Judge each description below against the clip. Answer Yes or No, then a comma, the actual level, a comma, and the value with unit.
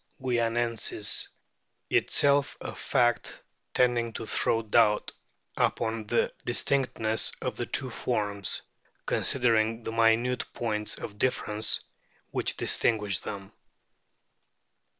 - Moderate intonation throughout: No, narrow, 2.1 semitones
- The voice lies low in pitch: Yes, low, 115 Hz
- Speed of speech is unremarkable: No, slow, 95 wpm